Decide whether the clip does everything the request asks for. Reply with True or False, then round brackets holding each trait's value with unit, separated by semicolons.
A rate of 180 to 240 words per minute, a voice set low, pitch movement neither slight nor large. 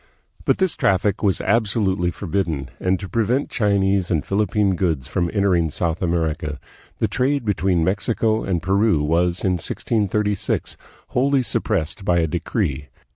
False (145 wpm; 95 Hz; 3.8 semitones)